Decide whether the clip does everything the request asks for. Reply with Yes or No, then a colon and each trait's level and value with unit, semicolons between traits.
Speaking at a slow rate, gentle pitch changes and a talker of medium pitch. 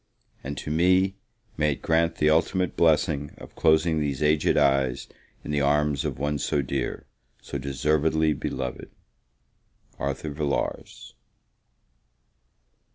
No: slow, 120 wpm; narrow, 2.0 semitones; very low, 75 Hz